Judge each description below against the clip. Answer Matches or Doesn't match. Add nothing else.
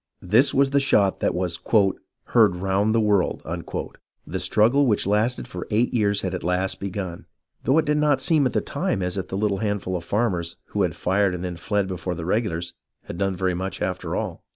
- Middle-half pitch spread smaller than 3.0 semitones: Doesn't match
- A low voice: Matches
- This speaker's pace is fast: Matches